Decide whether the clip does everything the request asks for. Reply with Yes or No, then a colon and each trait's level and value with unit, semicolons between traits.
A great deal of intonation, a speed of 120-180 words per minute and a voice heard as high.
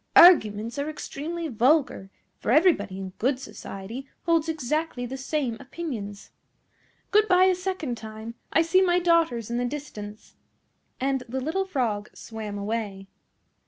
Yes: wide, 7.0 semitones; average, 140 wpm; very high, 265 Hz